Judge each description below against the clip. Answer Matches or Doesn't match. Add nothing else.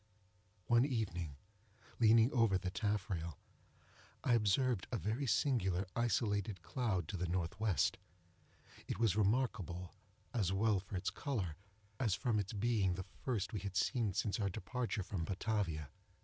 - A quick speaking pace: Doesn't match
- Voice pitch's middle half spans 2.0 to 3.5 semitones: Doesn't match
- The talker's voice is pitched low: Matches